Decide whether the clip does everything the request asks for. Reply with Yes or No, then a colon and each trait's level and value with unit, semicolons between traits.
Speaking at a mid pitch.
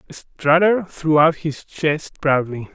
Yes: medium, 155 Hz